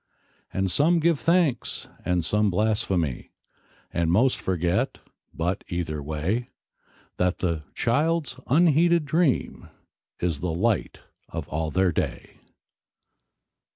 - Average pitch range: No, wide, 8.7 semitones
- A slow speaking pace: Yes, slow, 120 wpm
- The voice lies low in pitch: Yes, low, 100 Hz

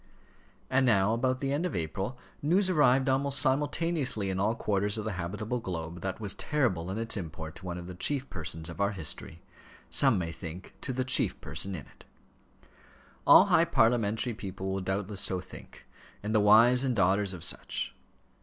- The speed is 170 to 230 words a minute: Yes, average, 185 wpm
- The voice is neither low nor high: No, low, 105 Hz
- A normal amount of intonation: No, wide, 5.7 semitones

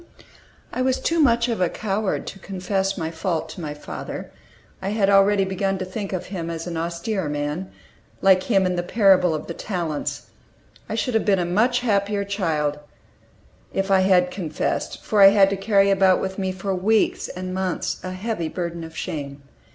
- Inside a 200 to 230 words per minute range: No, average, 190 wpm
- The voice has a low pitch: No, high, 190 Hz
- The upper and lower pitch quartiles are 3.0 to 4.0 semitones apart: No, narrow, 2.6 semitones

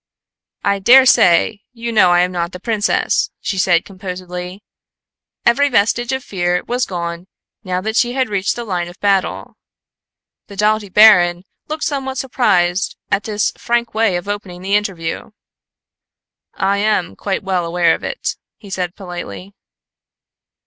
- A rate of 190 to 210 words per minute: No, average, 150 wpm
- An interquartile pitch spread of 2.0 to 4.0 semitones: Yes, average, 3.7 semitones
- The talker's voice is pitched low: No, high, 195 Hz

